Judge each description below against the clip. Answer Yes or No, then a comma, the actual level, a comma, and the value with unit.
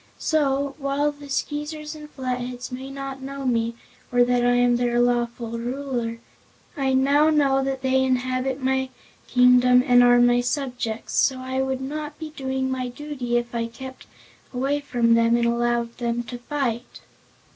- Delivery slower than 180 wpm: Yes, average, 165 wpm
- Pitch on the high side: Yes, very high, 255 Hz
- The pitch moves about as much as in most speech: No, narrow, 2.1 semitones